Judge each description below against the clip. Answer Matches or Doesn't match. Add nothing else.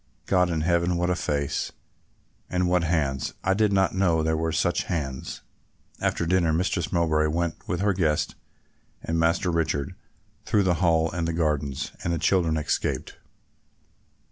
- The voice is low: Matches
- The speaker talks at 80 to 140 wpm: Doesn't match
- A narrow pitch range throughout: Matches